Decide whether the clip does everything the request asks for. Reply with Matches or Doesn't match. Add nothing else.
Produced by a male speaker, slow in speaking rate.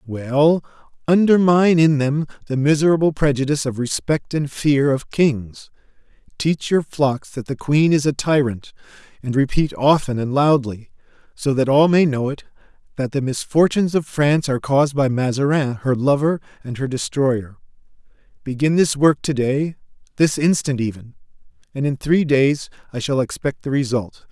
Doesn't match